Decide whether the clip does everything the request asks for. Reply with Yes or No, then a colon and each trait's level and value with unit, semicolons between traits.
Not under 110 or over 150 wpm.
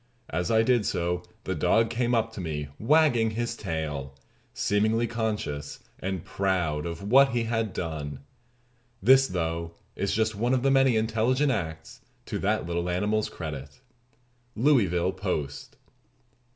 Yes: average, 140 wpm